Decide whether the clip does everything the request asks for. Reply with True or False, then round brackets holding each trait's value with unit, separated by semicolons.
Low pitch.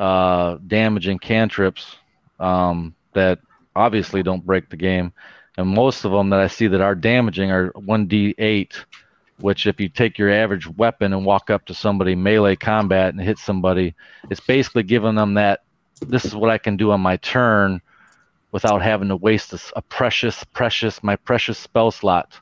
True (100 Hz)